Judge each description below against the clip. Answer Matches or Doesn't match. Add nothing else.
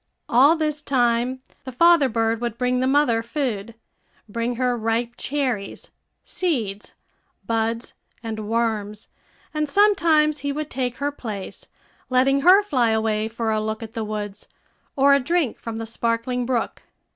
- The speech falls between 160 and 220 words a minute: Doesn't match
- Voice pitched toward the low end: Doesn't match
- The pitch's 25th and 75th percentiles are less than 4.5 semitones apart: Matches